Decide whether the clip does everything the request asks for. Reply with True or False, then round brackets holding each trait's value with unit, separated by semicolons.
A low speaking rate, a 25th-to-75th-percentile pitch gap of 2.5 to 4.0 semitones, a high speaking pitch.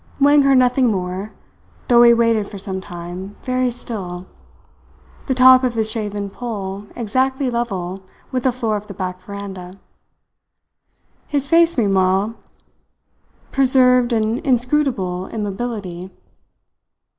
False (120 wpm; 4.7 semitones; 225 Hz)